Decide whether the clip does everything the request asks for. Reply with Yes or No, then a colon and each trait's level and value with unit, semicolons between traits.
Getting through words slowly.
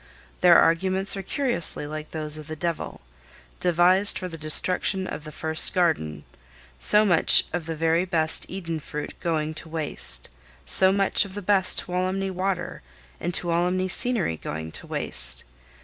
No: average, 150 wpm